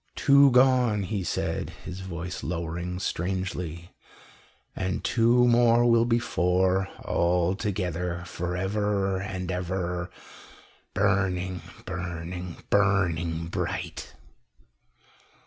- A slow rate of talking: Yes, slow, 95 wpm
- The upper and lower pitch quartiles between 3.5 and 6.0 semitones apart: No, average, 2.7 semitones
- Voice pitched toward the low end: Yes, very low, 95 Hz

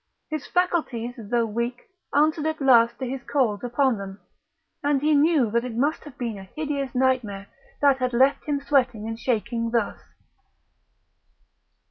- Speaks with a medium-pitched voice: No, very high, 250 Hz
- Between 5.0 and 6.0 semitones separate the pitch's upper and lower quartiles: No, average, 3.7 semitones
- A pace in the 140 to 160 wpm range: Yes, average, 155 wpm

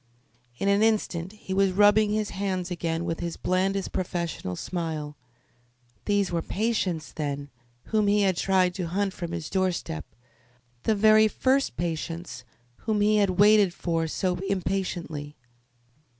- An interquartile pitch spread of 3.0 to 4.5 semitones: Yes, average, 3.3 semitones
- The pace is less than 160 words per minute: Yes, average, 140 wpm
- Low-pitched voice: No, medium, 185 Hz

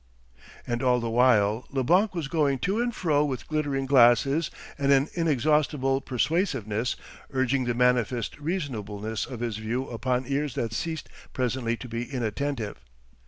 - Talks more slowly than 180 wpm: Yes, average, 145 wpm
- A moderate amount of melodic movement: Yes, average, 3.7 semitones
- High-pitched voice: No, low, 130 Hz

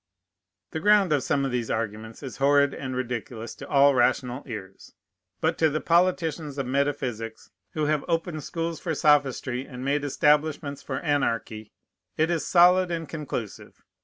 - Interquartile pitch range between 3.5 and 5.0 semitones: Yes, average, 4.1 semitones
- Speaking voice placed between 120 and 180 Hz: Yes, medium, 140 Hz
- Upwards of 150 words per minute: Yes, average, 160 wpm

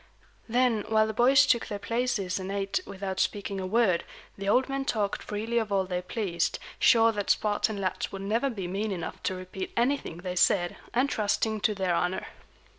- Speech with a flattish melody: No, average, 3.4 semitones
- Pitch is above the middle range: Yes, high, 205 Hz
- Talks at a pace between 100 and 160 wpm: No, average, 190 wpm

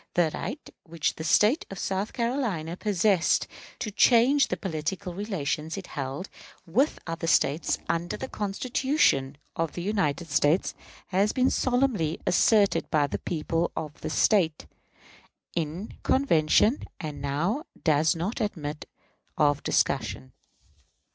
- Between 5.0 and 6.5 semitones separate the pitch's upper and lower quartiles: Yes, wide, 5.4 semitones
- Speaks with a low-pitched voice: No, medium, 175 Hz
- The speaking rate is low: Yes, slow, 130 wpm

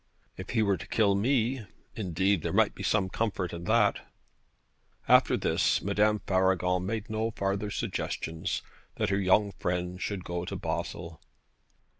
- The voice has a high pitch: No, low, 100 Hz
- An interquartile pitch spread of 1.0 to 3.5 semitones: Yes, average, 2.8 semitones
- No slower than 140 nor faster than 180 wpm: Yes, average, 150 wpm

